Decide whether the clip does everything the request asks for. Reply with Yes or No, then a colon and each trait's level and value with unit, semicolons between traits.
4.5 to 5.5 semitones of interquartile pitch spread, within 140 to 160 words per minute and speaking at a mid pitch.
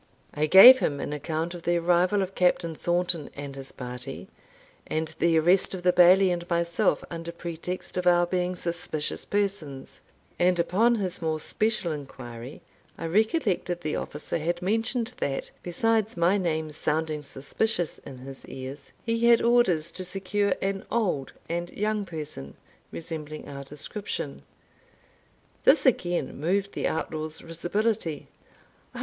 No: average, 3.9 semitones; average, 145 wpm; medium, 175 Hz